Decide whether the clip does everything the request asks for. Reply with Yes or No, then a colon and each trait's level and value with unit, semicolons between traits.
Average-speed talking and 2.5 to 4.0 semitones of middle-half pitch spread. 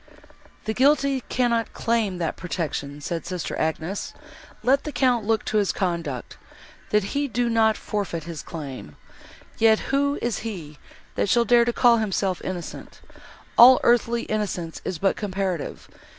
No: average, 145 wpm; wide, 5.6 semitones